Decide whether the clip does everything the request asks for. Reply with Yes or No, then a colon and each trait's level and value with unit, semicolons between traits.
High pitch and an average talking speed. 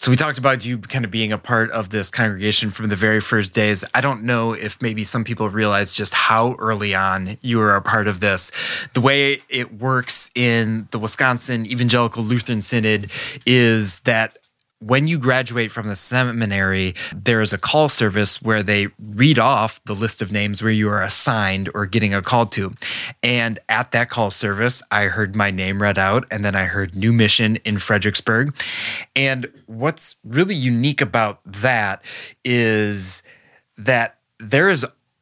No: low, 110 Hz; average, 180 wpm